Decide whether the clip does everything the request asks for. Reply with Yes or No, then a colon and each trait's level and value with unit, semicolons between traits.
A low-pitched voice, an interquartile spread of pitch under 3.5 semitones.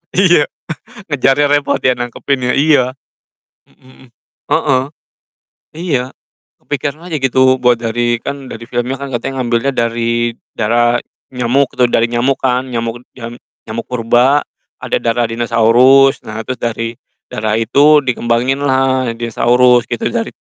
Yes: low, 125 Hz; narrow, 2.5 semitones